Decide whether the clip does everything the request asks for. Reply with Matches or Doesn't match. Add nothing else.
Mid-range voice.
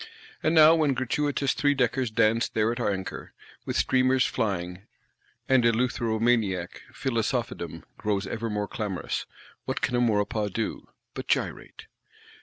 Doesn't match